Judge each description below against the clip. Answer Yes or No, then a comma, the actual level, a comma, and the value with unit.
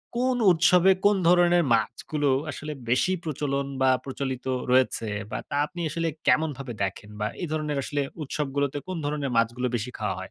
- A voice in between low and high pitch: Yes, medium, 145 Hz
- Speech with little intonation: No, average, 4.3 semitones